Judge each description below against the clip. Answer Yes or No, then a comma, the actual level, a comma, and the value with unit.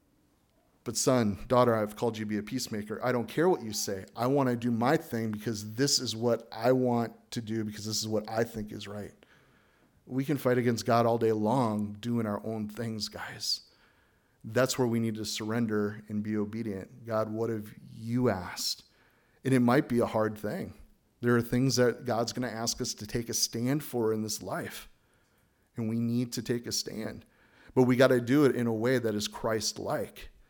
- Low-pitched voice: Yes, low, 115 Hz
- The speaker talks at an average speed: No, fast, 215 wpm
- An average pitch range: No, narrow, 2.3 semitones